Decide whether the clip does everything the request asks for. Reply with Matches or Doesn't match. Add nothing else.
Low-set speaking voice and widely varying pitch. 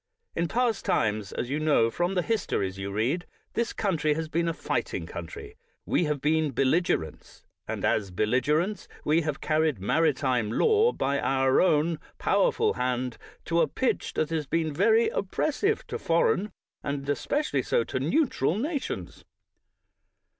Doesn't match